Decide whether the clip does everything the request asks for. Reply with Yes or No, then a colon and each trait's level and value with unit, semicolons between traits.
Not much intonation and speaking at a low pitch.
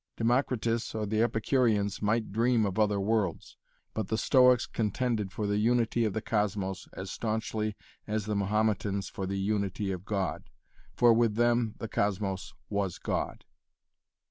Yes: narrow, 2.2 semitones; low, 105 Hz